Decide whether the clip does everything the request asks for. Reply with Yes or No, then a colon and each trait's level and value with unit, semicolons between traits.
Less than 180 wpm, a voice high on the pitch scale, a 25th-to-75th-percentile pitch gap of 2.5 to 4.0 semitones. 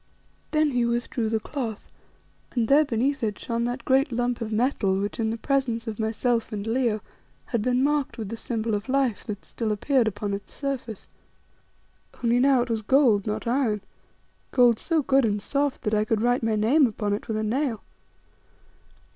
No: average, 190 wpm; high, 235 Hz; average, 3.4 semitones